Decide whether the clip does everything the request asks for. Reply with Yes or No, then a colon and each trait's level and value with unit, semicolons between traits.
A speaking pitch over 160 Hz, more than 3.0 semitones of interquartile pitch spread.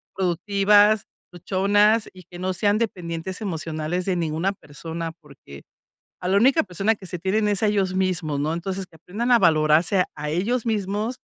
Yes: medium, 185 Hz; average, 3.7 semitones